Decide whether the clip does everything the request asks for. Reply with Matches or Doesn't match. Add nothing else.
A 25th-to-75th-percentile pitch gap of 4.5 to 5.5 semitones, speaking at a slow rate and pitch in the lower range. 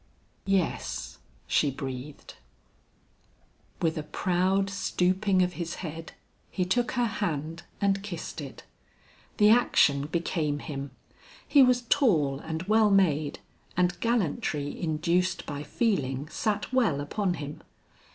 Doesn't match